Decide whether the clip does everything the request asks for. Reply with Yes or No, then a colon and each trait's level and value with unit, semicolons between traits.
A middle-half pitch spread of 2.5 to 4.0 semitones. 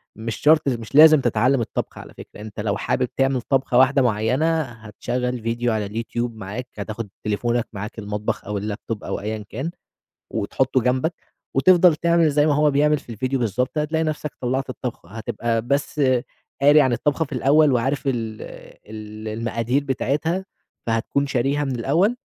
No: average, 4.4 semitones